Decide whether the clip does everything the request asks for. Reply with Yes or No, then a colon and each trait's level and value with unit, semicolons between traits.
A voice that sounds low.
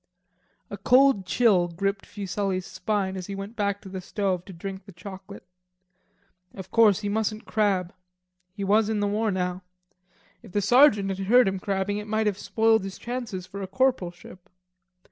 No: high, 200 Hz